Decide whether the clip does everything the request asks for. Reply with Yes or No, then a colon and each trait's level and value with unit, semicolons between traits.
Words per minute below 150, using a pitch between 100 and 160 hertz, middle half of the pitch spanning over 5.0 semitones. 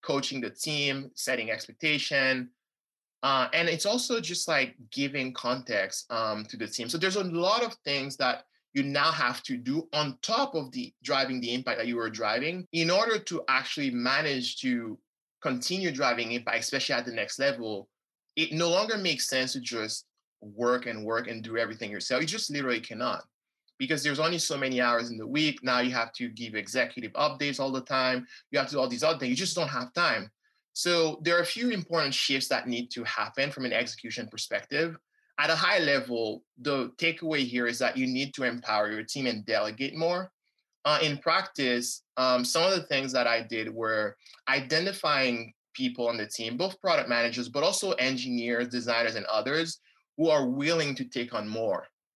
No: average, 195 wpm; low, 135 Hz; wide, 5.5 semitones